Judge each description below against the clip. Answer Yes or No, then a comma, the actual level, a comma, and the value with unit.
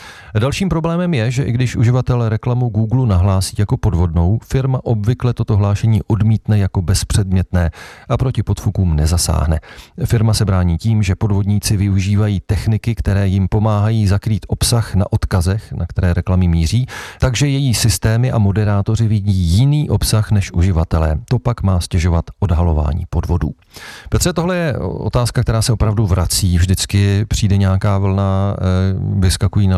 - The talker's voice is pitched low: Yes, low, 105 Hz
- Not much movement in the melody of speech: No, average, 3.6 semitones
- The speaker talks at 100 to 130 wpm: No, average, 145 wpm